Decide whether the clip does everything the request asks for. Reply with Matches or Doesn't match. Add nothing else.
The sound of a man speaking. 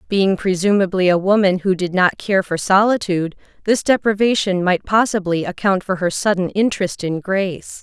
Doesn't match